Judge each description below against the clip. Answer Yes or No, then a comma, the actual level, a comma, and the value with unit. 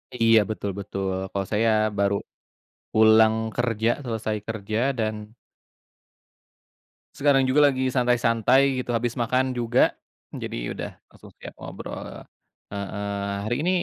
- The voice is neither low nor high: No, low, 115 Hz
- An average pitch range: Yes, average, 3.0 semitones